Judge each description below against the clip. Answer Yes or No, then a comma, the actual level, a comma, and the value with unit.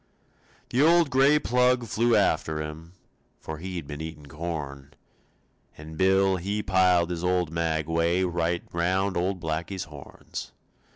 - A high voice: No, very low, 85 Hz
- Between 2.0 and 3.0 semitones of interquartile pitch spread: No, average, 3.4 semitones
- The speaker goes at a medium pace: No, slow, 130 wpm